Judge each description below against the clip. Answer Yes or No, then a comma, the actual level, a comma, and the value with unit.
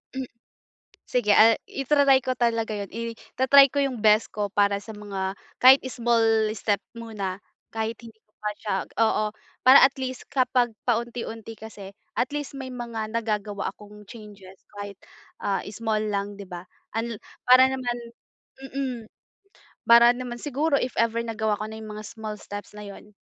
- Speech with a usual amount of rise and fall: Yes, average, 3.0 semitones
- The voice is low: No, high, 225 Hz